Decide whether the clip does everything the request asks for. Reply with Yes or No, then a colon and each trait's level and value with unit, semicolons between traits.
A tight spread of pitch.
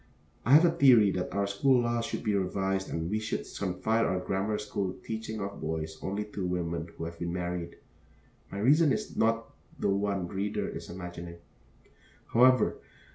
No: average, 3.9 semitones